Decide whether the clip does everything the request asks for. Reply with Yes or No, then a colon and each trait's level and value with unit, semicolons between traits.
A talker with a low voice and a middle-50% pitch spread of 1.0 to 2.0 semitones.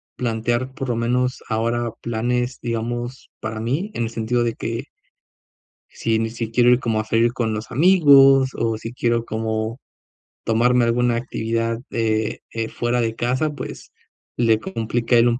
Yes: low, 115 Hz; narrow, 1.6 semitones